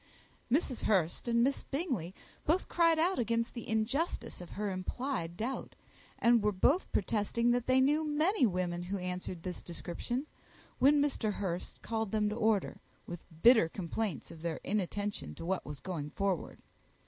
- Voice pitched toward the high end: Yes, high, 215 Hz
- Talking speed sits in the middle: Yes, average, 160 wpm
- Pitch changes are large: Yes, wide, 6.1 semitones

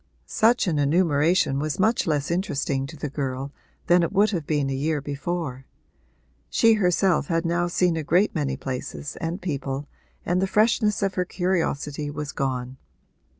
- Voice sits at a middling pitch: Yes, medium, 160 Hz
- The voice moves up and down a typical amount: Yes, average, 4.3 semitones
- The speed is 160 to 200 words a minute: Yes, average, 165 wpm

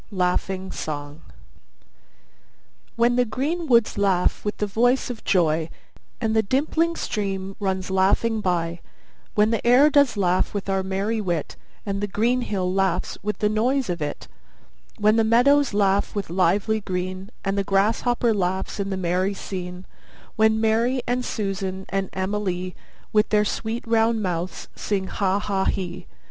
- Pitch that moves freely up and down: No, average, 3.1 semitones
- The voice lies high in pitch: Yes, high, 200 Hz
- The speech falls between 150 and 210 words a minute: Yes, average, 155 wpm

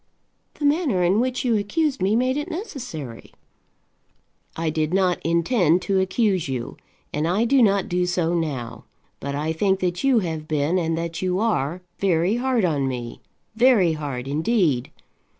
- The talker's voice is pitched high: No, medium, 180 Hz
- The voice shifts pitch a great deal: Yes, wide, 6.3 semitones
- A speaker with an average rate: Yes, average, 165 wpm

